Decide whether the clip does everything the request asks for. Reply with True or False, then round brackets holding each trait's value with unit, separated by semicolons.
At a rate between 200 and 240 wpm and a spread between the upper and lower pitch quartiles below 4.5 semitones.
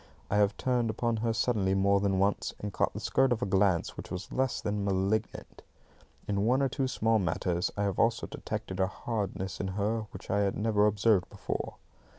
True (205 wpm; 2.8 semitones)